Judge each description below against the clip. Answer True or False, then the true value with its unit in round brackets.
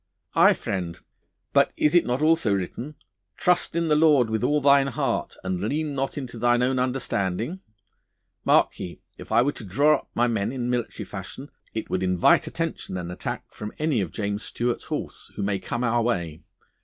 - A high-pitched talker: False (120 Hz)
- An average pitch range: False (5.9 semitones)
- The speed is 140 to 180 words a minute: False (190 wpm)